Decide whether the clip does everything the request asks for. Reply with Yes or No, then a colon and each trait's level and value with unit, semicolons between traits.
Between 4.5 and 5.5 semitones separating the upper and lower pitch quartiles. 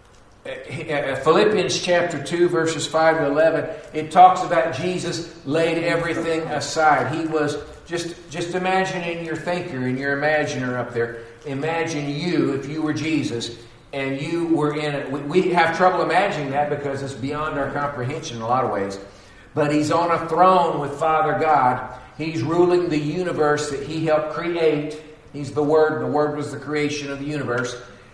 No: average, 2.8 semitones